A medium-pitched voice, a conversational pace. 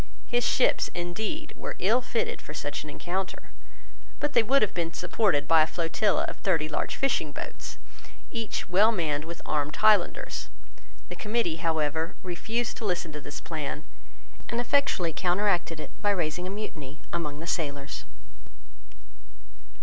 Yes: medium, 175 Hz; average, 150 wpm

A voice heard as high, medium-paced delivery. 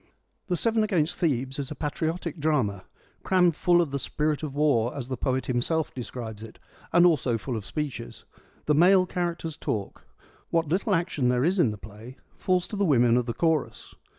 No: medium, 150 Hz; average, 195 wpm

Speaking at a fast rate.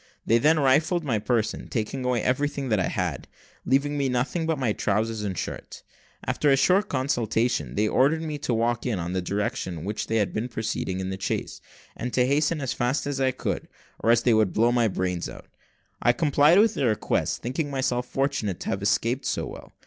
Yes: fast, 210 wpm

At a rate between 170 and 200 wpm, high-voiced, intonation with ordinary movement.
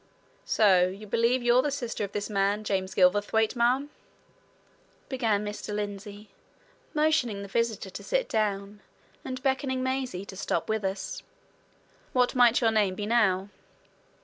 No: average, 145 wpm; high, 215 Hz; average, 3.7 semitones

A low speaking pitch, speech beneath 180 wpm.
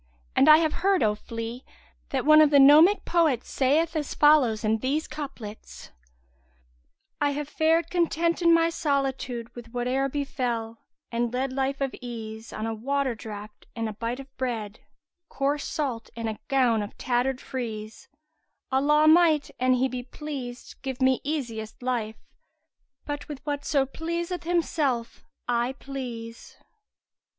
No: very high, 265 Hz; average, 155 wpm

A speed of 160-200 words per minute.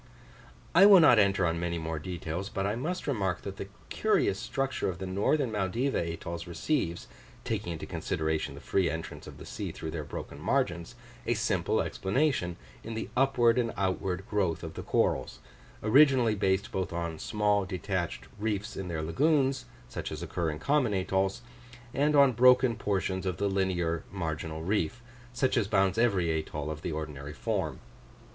Yes: average, 170 wpm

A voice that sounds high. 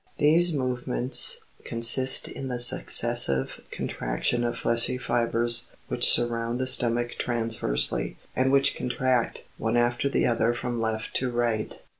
No: low, 120 Hz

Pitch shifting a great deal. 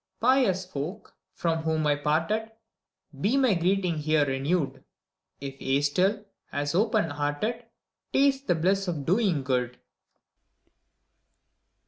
Yes: wide, 6.4 semitones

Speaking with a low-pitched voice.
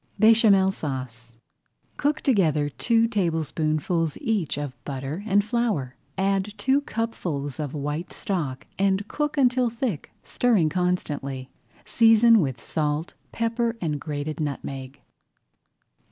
No: medium, 175 Hz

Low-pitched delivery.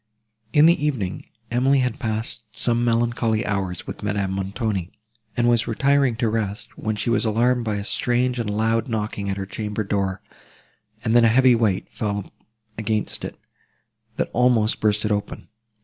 Yes: low, 110 Hz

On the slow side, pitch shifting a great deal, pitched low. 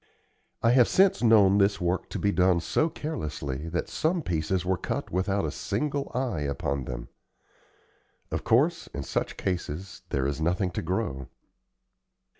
No: average, 155 wpm; wide, 6.8 semitones; very low, 95 Hz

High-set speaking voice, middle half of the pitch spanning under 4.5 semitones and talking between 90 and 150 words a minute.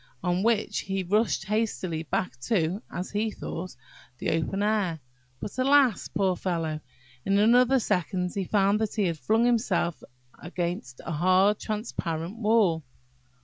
Yes: high, 195 Hz; average, 3.8 semitones; average, 145 wpm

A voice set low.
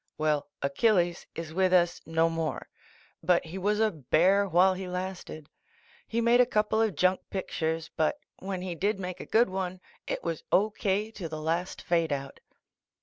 No: medium, 180 Hz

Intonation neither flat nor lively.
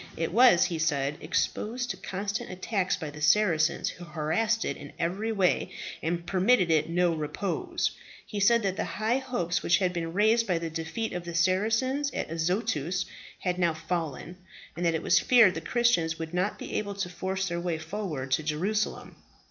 Yes: average, 4.5 semitones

